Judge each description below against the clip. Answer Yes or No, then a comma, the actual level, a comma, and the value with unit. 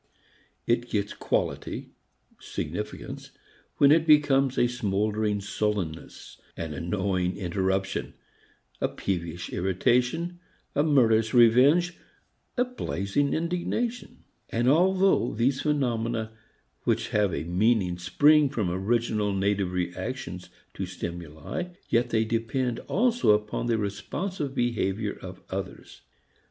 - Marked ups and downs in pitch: Yes, wide, 6.2 semitones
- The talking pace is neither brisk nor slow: No, slow, 105 wpm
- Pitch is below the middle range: Yes, low, 110 Hz